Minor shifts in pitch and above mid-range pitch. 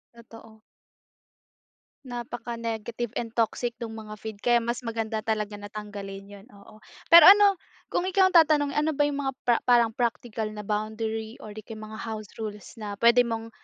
Yes: narrow, 2.1 semitones; high, 225 Hz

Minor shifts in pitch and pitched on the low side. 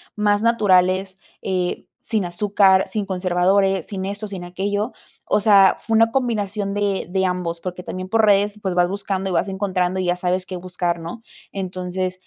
No: narrow, 2.0 semitones; high, 190 Hz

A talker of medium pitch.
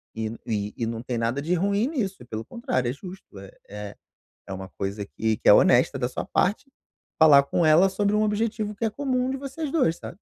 Yes: medium, 170 Hz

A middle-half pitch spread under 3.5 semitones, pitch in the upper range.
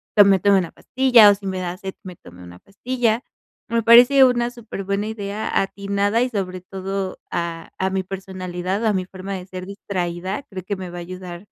Yes: narrow, 2.4 semitones; high, 195 Hz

